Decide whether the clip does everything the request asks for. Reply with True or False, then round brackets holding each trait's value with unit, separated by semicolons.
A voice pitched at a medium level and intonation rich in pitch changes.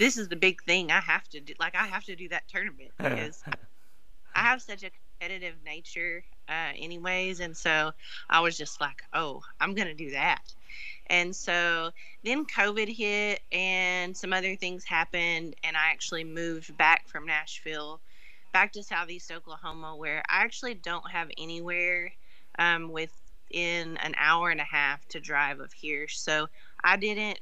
False (170 Hz; 2.7 semitones)